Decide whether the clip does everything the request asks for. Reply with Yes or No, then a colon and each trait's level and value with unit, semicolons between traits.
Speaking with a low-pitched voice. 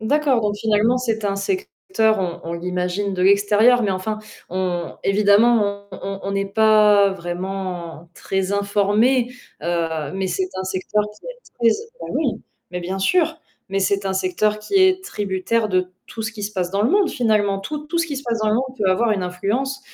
No: high, 205 Hz